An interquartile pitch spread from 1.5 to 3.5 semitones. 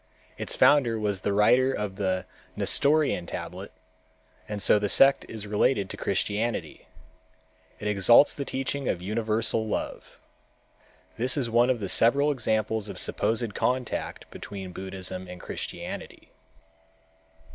No: average, 3.9 semitones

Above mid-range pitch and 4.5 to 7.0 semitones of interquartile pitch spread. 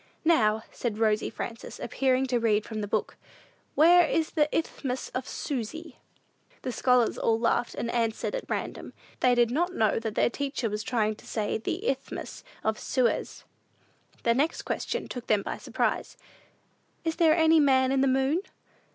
Yes: very high, 250 Hz; average, 5.1 semitones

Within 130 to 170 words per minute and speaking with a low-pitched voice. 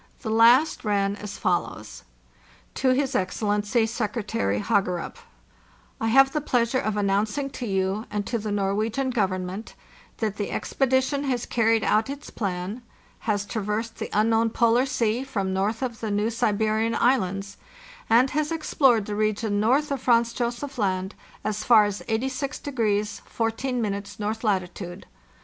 No: average, 145 wpm; high, 220 Hz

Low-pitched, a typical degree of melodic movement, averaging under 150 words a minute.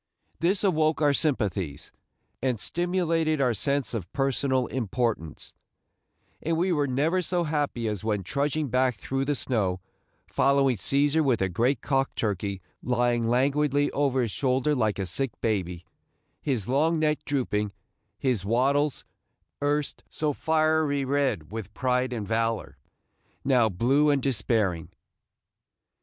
Yes: low, 130 Hz; average, 4.6 semitones; slow, 135 wpm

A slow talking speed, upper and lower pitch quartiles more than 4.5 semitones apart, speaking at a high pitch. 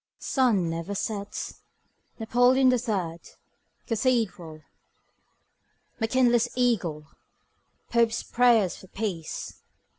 Yes: slow, 80 wpm; average, 5.3 semitones; high, 225 Hz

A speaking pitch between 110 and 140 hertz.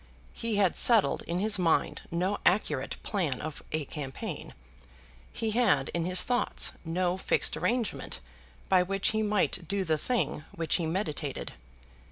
No: medium, 185 Hz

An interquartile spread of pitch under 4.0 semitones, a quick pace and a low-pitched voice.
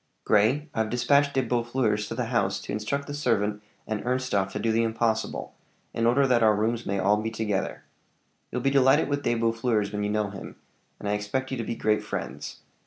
Yes: average, 3.3 semitones; fast, 210 wpm; low, 115 Hz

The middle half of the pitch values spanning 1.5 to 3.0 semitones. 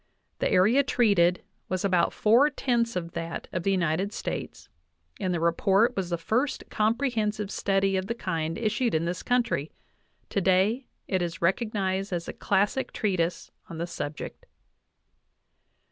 No: average, 4.3 semitones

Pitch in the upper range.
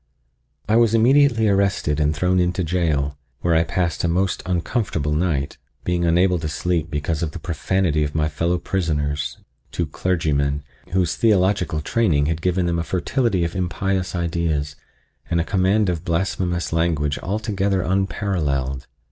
No: very low, 85 Hz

